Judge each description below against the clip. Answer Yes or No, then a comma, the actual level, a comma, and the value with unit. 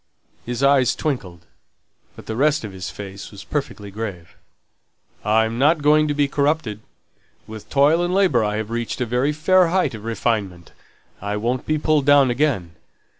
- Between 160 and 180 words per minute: Yes, average, 165 wpm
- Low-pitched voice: Yes, low, 125 Hz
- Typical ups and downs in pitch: No, wide, 5.8 semitones